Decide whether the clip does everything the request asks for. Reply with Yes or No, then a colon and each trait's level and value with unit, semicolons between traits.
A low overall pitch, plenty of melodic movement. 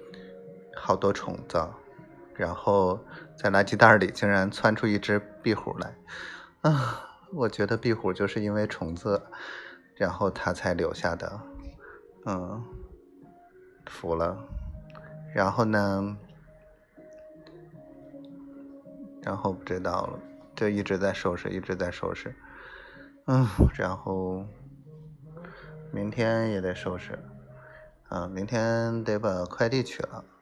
Yes: low, 105 Hz; wide, 8.6 semitones